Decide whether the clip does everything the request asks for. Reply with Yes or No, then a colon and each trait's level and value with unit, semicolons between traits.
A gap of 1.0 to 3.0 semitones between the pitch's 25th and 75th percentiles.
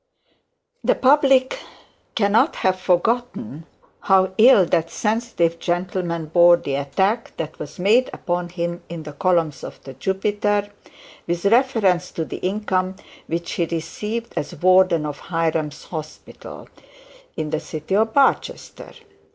No: average, 4.1 semitones